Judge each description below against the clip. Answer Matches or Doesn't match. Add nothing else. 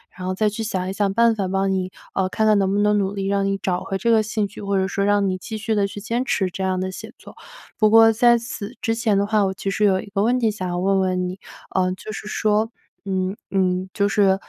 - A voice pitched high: Matches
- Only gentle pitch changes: Matches